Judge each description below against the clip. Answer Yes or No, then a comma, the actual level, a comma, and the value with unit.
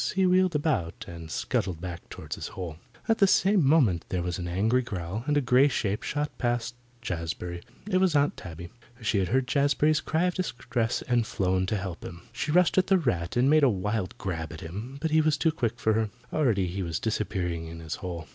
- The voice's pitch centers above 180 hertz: No, low, 110 Hz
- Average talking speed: No, fast, 220 wpm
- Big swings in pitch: Yes, wide, 8.8 semitones